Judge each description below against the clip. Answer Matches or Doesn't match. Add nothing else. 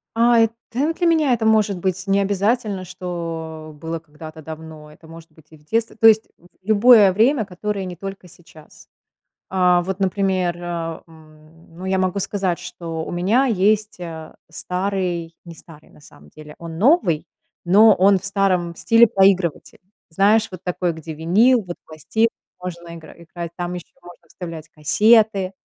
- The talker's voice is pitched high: Doesn't match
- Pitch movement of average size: Matches